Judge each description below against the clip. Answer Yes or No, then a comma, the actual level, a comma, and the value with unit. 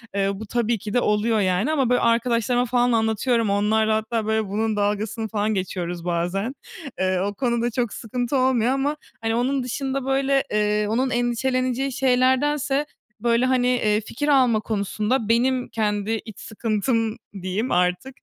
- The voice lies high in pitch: Yes, high, 230 Hz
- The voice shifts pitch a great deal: No, average, 3.3 semitones